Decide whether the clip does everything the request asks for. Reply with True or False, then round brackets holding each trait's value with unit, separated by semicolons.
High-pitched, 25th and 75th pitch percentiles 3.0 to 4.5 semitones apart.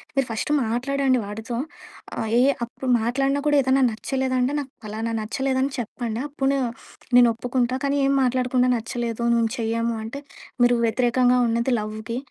False (245 Hz; 2.5 semitones)